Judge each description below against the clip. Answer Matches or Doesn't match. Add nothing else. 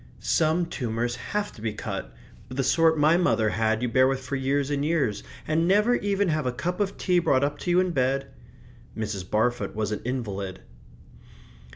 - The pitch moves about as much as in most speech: Doesn't match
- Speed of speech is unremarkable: Matches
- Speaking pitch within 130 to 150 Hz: Matches